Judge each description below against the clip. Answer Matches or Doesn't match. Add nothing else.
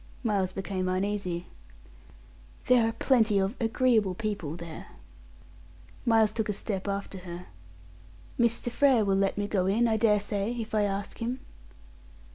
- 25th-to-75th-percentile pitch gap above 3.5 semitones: Doesn't match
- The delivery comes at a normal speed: Matches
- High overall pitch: Matches